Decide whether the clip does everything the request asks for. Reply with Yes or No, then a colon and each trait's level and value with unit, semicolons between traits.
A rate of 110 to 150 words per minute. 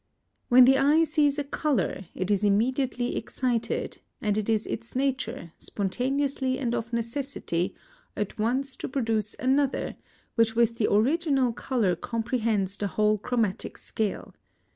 Yes: average, 140 wpm